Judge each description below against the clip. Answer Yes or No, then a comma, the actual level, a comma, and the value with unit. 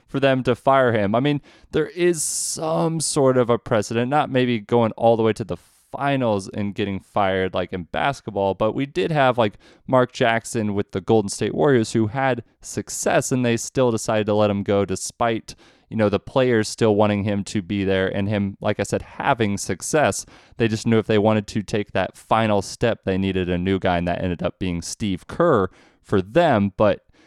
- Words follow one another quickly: Yes, fast, 210 wpm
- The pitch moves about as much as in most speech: Yes, average, 3.9 semitones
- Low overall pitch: Yes, low, 110 Hz